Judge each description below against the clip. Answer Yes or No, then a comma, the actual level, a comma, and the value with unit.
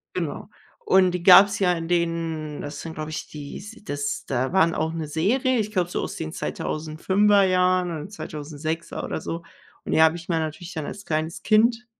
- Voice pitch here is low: No, medium, 165 Hz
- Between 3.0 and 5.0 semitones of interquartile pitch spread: Yes, average, 3.4 semitones